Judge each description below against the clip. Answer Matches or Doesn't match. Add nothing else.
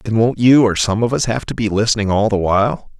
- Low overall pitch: Matches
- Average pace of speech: Doesn't match